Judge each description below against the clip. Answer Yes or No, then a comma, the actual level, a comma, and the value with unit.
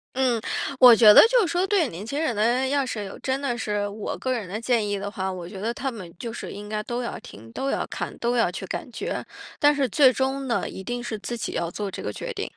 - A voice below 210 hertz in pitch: No, high, 235 Hz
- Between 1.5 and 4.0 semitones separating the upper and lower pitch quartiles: No, average, 4.4 semitones